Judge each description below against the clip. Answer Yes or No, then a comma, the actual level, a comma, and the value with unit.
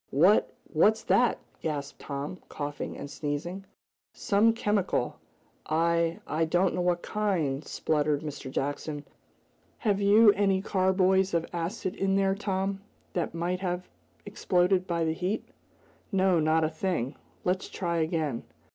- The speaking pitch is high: No, medium, 175 Hz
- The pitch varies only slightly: No, average, 3.6 semitones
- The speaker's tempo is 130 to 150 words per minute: Yes, slow, 135 wpm